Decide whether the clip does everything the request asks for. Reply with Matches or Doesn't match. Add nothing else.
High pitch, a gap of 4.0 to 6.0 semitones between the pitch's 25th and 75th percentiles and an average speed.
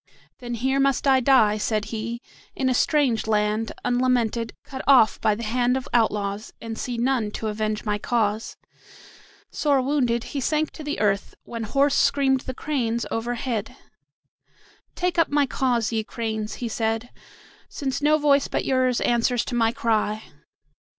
Doesn't match